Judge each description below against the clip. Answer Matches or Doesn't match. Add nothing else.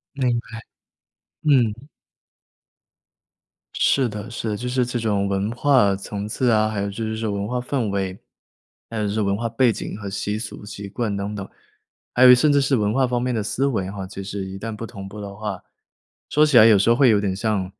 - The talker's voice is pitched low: Matches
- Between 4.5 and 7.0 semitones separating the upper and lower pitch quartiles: Doesn't match